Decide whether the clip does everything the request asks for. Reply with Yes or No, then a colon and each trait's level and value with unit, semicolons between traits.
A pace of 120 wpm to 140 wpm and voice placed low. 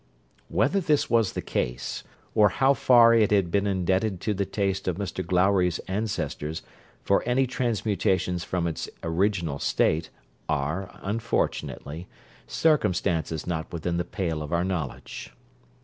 Yes: slow, 135 wpm; very low, 95 Hz